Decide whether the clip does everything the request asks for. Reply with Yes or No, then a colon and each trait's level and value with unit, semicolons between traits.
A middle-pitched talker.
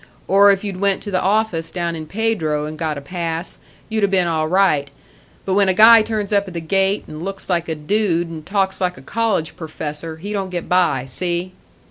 Yes: medium, 180 Hz